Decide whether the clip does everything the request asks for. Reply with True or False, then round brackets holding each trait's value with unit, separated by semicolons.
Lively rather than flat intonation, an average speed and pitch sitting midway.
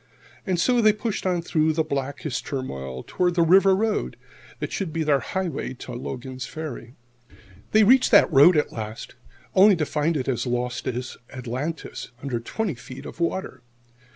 True (6.2 semitones; 170 wpm; 150 Hz)